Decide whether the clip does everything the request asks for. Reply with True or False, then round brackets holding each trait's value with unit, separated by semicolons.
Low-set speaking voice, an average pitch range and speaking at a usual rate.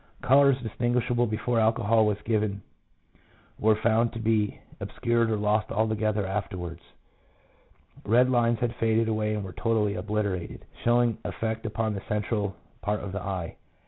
False (110 Hz; 1.9 semitones; 150 wpm)